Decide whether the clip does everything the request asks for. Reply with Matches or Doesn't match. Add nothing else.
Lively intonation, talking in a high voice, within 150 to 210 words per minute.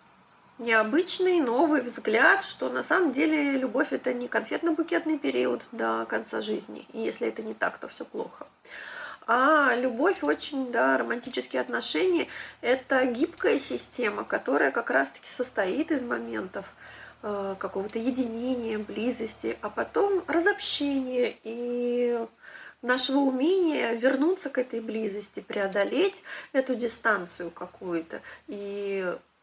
Doesn't match